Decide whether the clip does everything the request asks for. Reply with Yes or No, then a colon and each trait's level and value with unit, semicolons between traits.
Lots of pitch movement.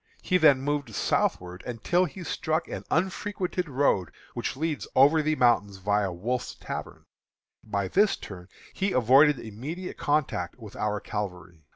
Yes: wide, 7.6 semitones